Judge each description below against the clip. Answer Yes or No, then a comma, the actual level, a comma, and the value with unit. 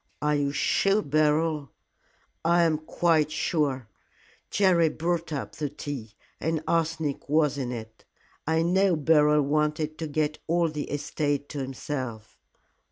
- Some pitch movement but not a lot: No, narrow, 2.2 semitones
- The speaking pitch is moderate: Yes, medium, 150 Hz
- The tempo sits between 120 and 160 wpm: Yes, average, 140 wpm